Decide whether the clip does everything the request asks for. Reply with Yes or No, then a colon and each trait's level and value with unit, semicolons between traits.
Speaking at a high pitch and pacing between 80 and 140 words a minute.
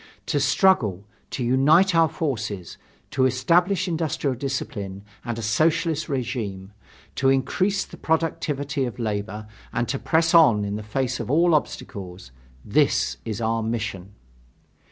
No: low, 130 Hz; slow, 135 wpm